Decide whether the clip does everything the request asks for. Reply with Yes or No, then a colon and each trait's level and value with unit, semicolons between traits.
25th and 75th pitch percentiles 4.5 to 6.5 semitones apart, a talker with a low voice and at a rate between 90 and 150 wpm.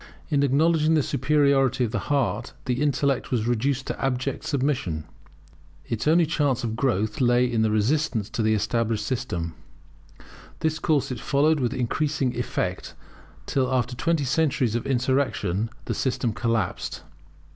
No: average, 3.7 semitones; low, 130 Hz; average, 145 wpm